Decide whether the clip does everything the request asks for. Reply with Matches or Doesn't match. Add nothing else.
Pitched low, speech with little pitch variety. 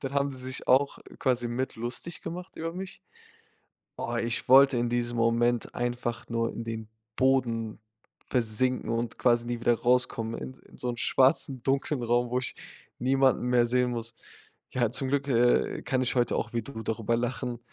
Matches